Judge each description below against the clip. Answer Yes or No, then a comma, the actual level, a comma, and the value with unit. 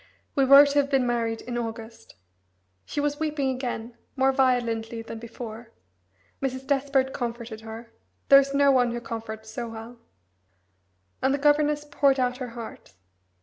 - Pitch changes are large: No, average, 3.2 semitones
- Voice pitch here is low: No, very high, 250 Hz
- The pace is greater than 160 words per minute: No, average, 155 wpm